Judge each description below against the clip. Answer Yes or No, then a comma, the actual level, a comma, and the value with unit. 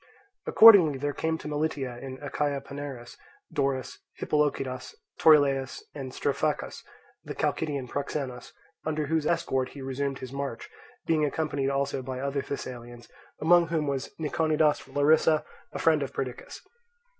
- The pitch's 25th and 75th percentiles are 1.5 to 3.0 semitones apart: Yes, narrow, 2.5 semitones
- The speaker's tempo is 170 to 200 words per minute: No, slow, 135 wpm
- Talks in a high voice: No, medium, 140 Hz